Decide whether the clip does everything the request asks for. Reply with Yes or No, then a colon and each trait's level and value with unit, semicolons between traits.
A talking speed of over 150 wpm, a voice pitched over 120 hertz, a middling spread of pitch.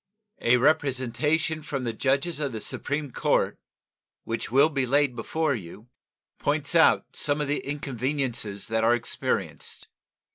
No: average, 140 wpm; low, 135 Hz; average, 3.8 semitones